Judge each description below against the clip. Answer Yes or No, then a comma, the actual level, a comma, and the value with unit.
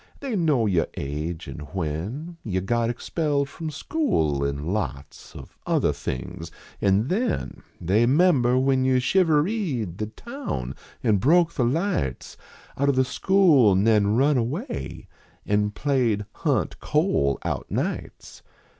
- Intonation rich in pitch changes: Yes, wide, 8.7 semitones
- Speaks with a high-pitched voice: No, low, 120 Hz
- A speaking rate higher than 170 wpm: No, average, 145 wpm